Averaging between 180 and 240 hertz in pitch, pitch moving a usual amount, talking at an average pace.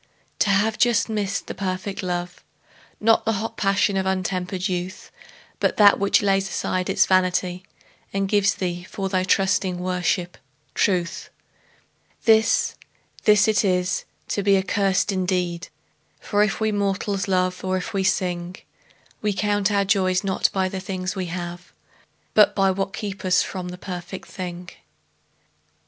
No: high, 190 Hz; narrow, 1.7 semitones; average, 150 wpm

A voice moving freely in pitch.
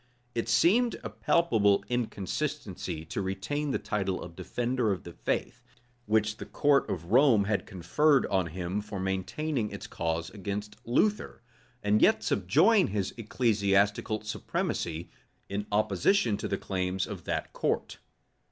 No: average, 4.5 semitones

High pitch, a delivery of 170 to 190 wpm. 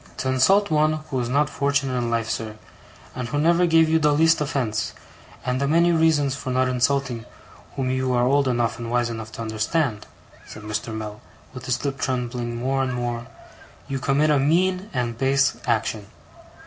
No: low, 130 Hz; average, 185 wpm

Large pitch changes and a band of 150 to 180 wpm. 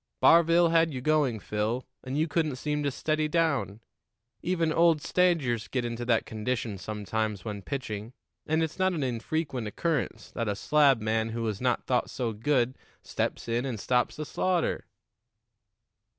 Yes: wide, 5.7 semitones; average, 160 wpm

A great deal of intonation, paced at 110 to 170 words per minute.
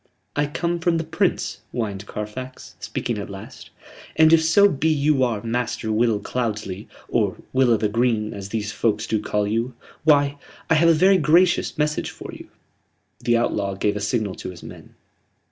No: wide, 6.5 semitones; average, 180 wpm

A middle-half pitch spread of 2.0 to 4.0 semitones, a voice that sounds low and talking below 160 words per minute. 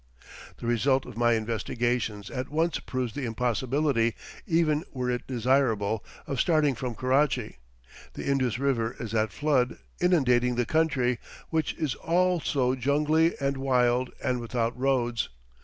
Yes: average, 3.1 semitones; low, 125 Hz; average, 140 wpm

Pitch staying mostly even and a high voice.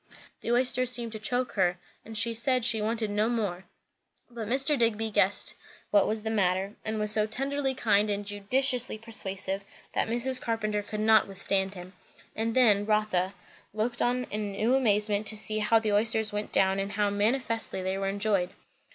Yes: narrow, 2.3 semitones; high, 215 Hz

